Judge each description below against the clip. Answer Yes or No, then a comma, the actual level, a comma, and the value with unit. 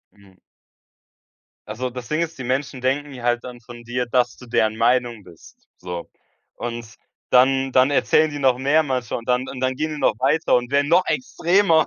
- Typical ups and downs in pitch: Yes, average, 3.1 semitones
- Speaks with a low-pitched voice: Yes, low, 130 Hz